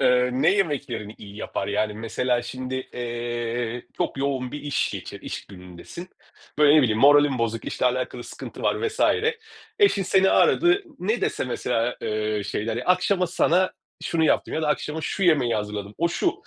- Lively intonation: Yes, wide, 5.8 semitones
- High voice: No, low, 125 Hz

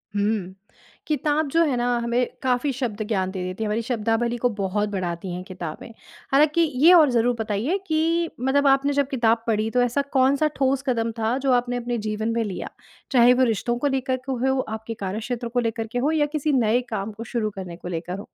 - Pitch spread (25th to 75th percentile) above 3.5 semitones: Yes, average, 3.9 semitones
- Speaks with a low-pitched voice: No, high, 235 Hz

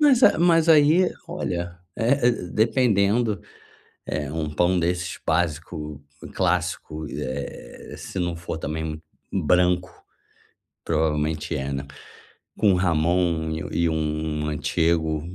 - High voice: No, very low, 85 Hz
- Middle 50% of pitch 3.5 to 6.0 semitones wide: Yes, average, 4.2 semitones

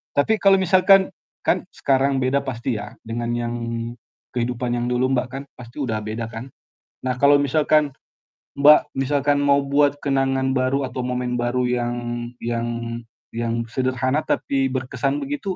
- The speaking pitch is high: No, low, 130 Hz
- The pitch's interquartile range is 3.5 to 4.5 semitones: No, average, 2.7 semitones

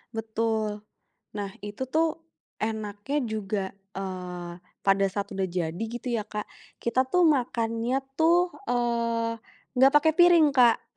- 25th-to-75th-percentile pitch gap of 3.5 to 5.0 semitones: Yes, average, 4.1 semitones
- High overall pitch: Yes, high, 230 Hz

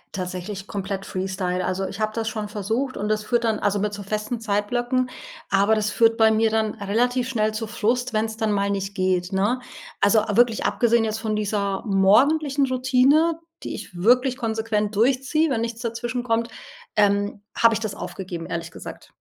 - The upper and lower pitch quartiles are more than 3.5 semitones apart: No, average, 3.0 semitones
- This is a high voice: Yes, high, 215 Hz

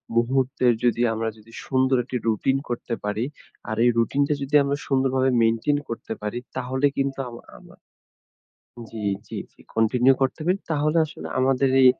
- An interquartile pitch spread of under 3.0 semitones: Yes, narrow, 2.6 semitones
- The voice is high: No, low, 130 Hz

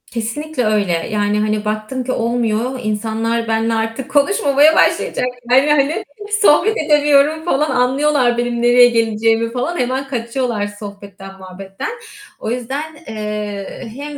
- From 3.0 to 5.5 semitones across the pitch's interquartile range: Yes, average, 4.3 semitones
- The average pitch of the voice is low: No, high, 240 Hz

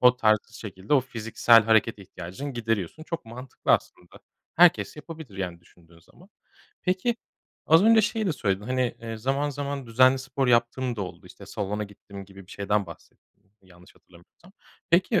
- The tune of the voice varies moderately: No, wide, 6.2 semitones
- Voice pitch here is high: No, low, 115 Hz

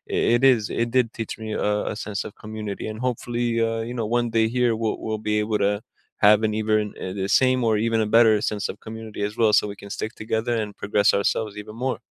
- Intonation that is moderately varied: No, narrow, 1.5 semitones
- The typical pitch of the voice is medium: No, low, 110 Hz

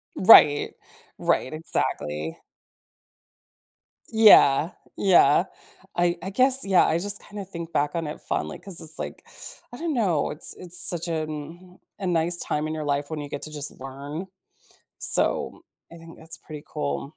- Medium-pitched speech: Yes, medium, 165 Hz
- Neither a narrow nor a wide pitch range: Yes, average, 3.8 semitones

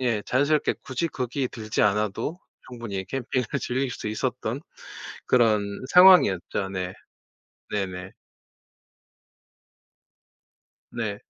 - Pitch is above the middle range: No, low, 115 Hz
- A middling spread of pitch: Yes, average, 4.7 semitones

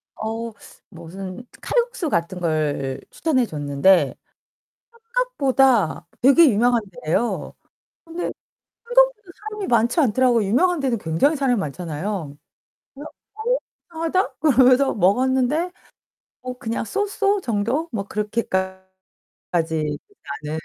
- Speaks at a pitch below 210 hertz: No, high, 240 Hz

